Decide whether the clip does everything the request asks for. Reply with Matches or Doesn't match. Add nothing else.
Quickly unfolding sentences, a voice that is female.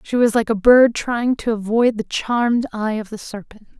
Matches